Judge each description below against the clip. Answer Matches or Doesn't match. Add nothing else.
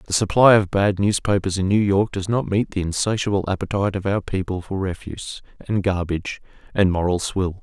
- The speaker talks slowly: Doesn't match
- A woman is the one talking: Doesn't match